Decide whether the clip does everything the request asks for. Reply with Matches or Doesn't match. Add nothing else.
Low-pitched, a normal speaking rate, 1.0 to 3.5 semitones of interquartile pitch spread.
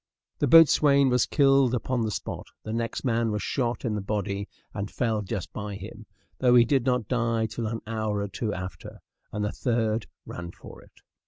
Matches